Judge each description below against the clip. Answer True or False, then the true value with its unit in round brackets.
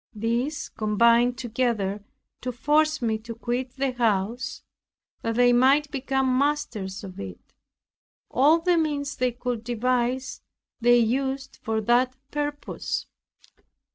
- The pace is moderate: False (120 wpm)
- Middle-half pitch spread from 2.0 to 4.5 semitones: True (2.9 semitones)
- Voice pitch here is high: True (245 Hz)